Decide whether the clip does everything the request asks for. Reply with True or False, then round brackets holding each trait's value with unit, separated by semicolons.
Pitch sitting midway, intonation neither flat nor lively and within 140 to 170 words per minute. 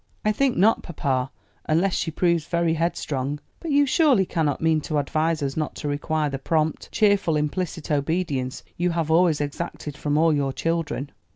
False (160 Hz; 3.0 semitones; 180 wpm)